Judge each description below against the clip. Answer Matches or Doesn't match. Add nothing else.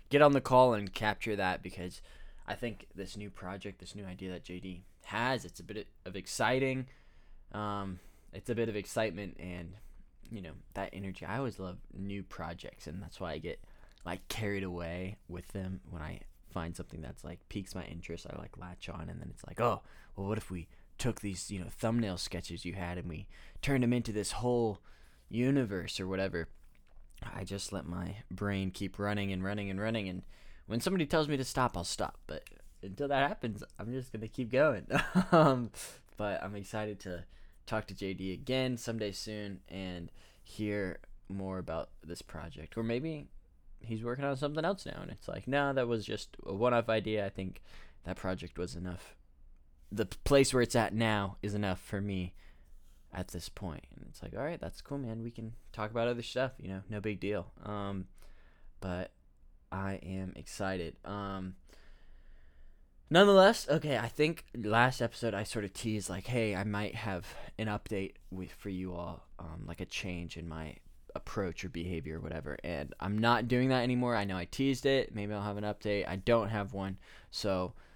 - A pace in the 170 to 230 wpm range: Matches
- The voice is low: Matches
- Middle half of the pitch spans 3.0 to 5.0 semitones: Matches